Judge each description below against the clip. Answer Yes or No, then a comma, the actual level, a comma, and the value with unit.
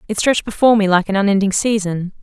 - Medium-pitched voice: No, high, 205 Hz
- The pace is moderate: No, fast, 215 wpm